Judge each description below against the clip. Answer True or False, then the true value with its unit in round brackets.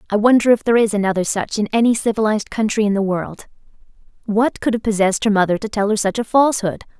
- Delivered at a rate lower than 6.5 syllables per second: False (6.8 syllables/s)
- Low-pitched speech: False (215 Hz)